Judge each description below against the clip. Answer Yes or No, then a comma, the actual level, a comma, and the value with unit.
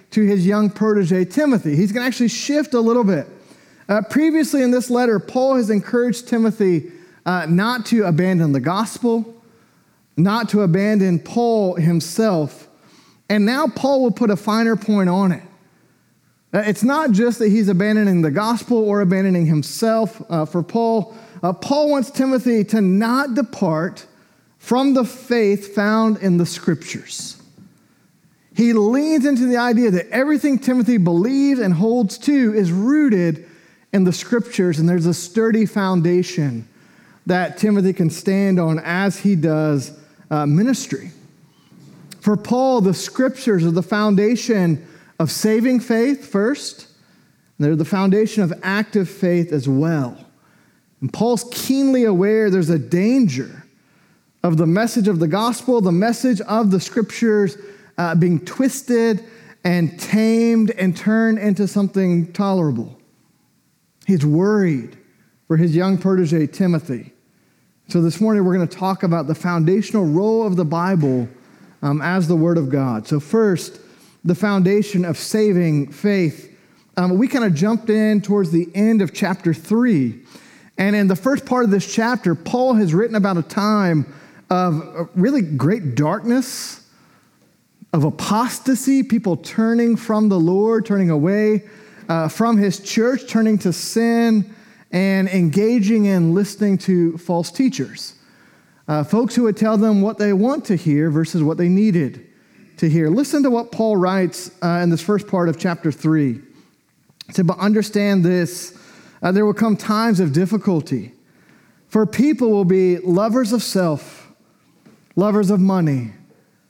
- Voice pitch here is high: Yes, high, 200 Hz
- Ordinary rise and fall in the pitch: Yes, average, 4.4 semitones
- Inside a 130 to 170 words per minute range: Yes, average, 150 wpm